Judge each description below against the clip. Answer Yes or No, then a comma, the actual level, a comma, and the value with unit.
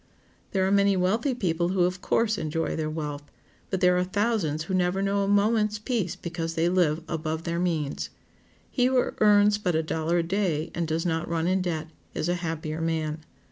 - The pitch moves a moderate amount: Yes, average, 3.5 semitones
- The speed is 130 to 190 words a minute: No, average, 200 wpm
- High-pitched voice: No, medium, 175 Hz